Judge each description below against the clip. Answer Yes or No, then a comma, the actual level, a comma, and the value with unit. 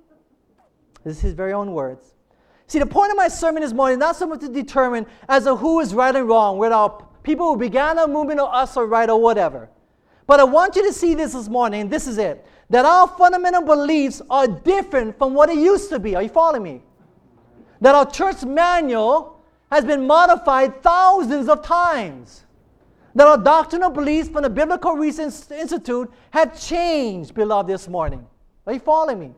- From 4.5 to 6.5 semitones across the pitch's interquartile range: Yes, average, 5.3 semitones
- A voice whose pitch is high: Yes, very high, 290 Hz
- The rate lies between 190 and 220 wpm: Yes, average, 195 wpm